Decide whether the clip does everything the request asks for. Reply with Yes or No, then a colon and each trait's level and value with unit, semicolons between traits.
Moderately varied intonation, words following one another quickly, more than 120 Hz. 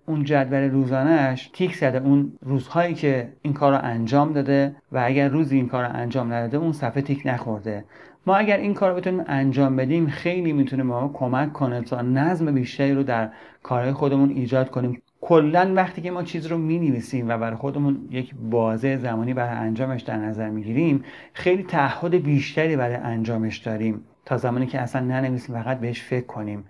Yes: average, 3.3 semitones; fast, 180 wpm; low, 135 Hz